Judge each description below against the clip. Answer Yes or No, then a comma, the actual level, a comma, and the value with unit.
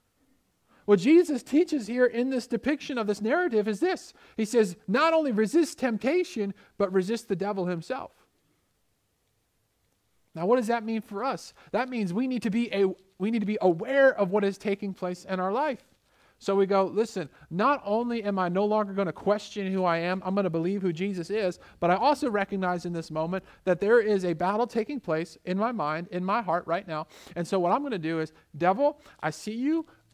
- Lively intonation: No, average, 4.8 semitones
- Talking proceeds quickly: Yes, fast, 210 wpm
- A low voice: No, high, 200 Hz